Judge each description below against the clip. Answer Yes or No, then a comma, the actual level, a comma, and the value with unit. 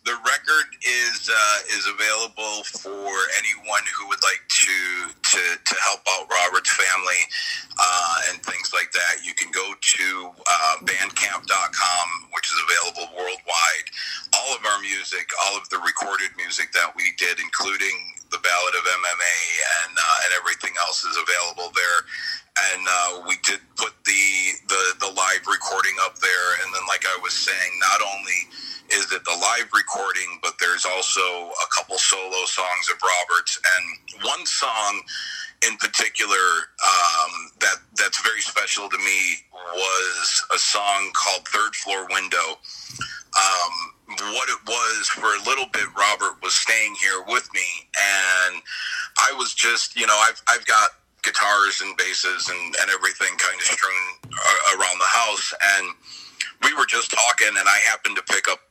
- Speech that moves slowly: No, average, 160 wpm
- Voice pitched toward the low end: Yes, low, 105 Hz